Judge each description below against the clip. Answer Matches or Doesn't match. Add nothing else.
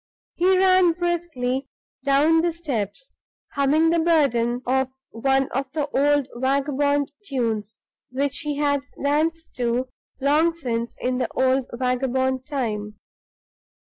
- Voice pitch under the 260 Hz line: Doesn't match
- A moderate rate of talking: Doesn't match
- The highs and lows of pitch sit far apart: Doesn't match